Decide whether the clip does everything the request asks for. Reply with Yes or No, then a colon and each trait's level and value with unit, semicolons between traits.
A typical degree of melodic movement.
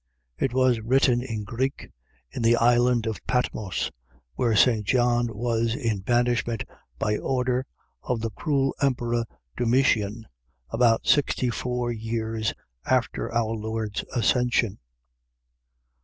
No: narrow, 1.8 semitones